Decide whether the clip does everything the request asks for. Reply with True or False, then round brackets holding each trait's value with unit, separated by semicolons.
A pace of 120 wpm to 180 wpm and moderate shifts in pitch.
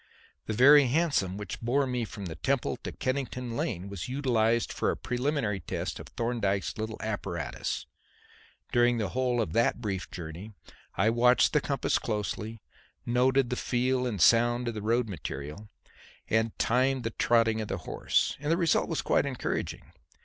True (165 wpm; 3.2 semitones)